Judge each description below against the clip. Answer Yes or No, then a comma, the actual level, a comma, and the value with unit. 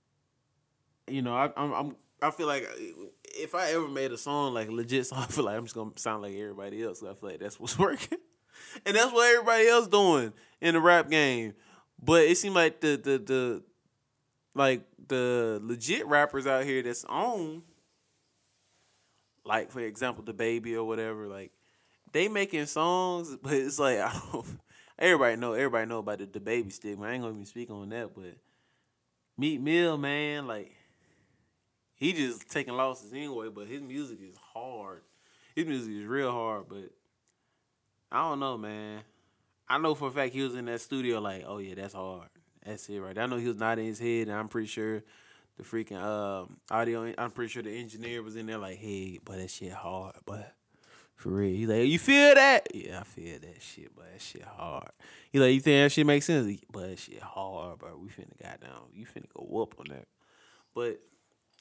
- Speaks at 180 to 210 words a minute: Yes, average, 200 wpm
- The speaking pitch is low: Yes, low, 120 Hz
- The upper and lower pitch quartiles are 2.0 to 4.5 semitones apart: No, average, 5.0 semitones